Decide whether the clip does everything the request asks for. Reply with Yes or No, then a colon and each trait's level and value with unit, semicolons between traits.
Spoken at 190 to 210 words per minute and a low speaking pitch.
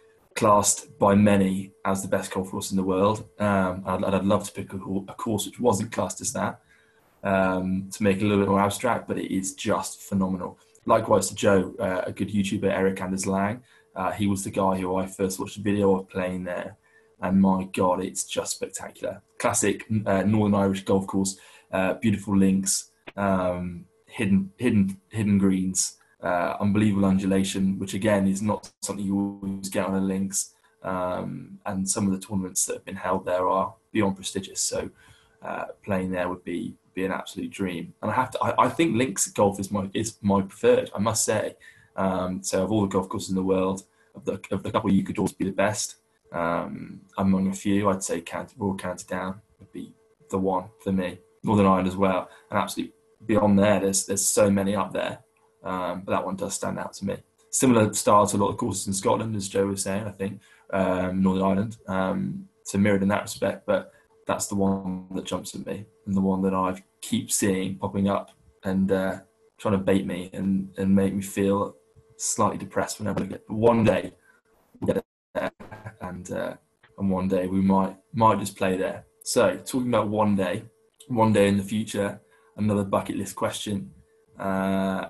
Yes: fast, 205 wpm; very low, 95 Hz